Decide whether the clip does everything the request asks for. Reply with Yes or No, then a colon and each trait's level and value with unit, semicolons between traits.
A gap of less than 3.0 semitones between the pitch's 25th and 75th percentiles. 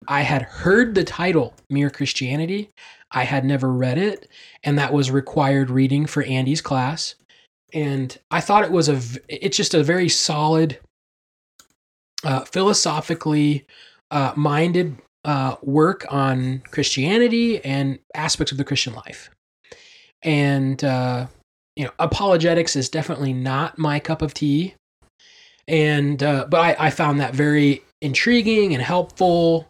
No: average, 3.8 semitones